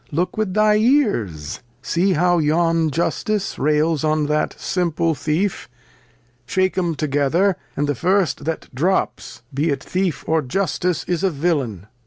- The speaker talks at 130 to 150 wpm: Yes, average, 145 wpm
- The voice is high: No, medium, 165 Hz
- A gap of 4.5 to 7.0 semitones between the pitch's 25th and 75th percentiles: No, average, 4.0 semitones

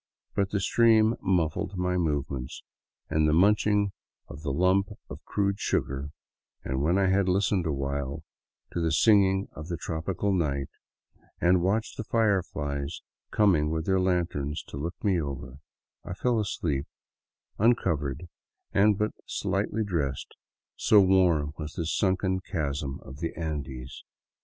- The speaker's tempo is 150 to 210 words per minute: No, average, 140 wpm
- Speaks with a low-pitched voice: Yes, very low, 85 Hz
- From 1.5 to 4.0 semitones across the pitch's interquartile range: No, average, 5.1 semitones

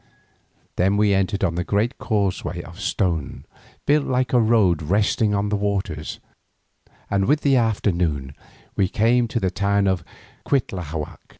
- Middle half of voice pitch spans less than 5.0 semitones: Yes, average, 3.9 semitones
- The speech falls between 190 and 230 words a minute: No, average, 145 wpm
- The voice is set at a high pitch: No, low, 100 Hz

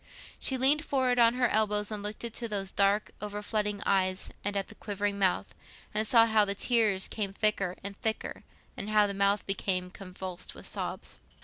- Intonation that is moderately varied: No, narrow, 1.8 semitones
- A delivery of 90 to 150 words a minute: No, average, 185 wpm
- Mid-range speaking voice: No, high, 205 Hz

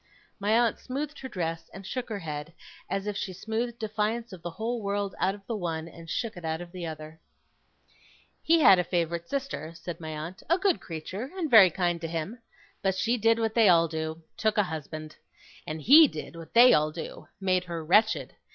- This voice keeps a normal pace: No, fast, 210 wpm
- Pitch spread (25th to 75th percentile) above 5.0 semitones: Yes, wide, 5.4 semitones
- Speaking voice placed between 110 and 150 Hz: No, medium, 185 Hz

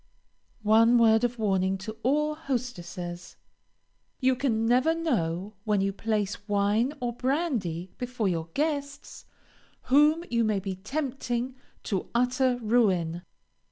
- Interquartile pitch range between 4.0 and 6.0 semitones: Yes, average, 4.7 semitones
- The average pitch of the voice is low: No, high, 230 Hz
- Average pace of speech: No, slow, 120 wpm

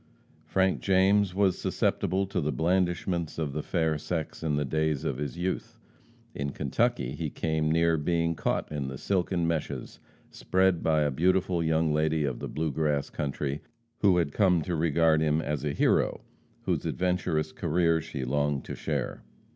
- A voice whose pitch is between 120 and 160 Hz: No, very low, 80 Hz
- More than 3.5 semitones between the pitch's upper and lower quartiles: No, average, 3.0 semitones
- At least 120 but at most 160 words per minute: No, average, 170 wpm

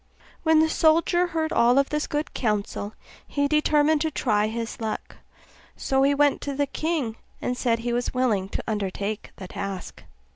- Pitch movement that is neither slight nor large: No, wide, 5.7 semitones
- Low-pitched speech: No, very high, 260 Hz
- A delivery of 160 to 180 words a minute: Yes, average, 170 wpm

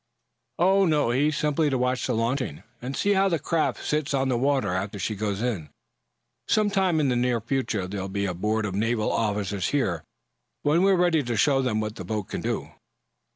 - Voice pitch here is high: No, low, 125 Hz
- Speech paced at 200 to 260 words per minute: Yes, fast, 205 wpm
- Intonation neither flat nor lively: No, wide, 6.2 semitones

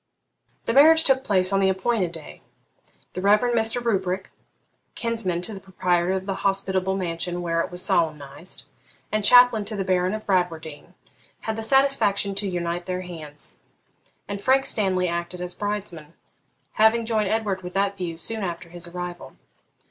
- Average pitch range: Yes, average, 3.4 semitones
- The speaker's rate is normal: Yes, average, 165 wpm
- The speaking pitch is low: No, high, 190 Hz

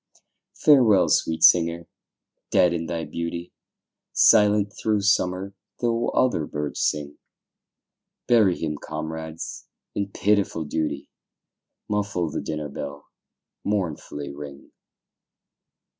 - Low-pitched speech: Yes, very low, 85 Hz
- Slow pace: Yes, slow, 100 wpm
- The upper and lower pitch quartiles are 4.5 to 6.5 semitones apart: Yes, average, 4.8 semitones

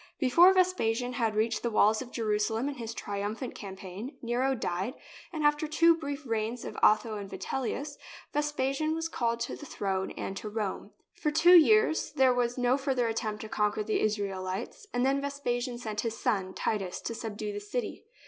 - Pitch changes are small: No, average, 4.8 semitones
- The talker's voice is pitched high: Yes, high, 235 Hz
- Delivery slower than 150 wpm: No, average, 185 wpm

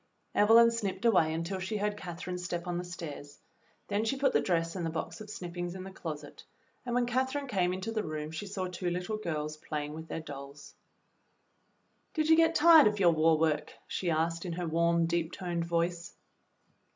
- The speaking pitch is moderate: Yes, medium, 175 Hz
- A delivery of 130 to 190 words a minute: No, average, 200 wpm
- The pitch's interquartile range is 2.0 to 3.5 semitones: No, average, 4.1 semitones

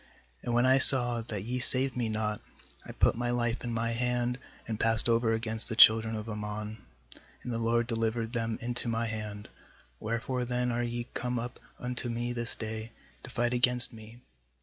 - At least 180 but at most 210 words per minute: Yes, average, 190 wpm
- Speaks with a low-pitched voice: Yes, low, 115 Hz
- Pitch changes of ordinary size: No, narrow, 1.5 semitones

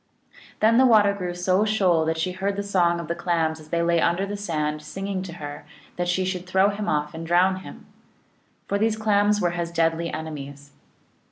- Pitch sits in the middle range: Yes, medium, 175 Hz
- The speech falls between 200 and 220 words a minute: Yes, fast, 205 wpm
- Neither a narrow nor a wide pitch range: Yes, average, 3.6 semitones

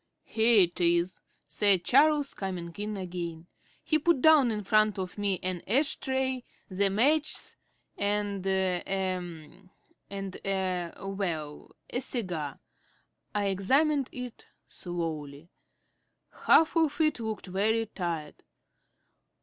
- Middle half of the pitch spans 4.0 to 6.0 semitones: Yes, average, 5.2 semitones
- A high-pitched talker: Yes, high, 195 Hz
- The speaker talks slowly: Yes, slow, 115 wpm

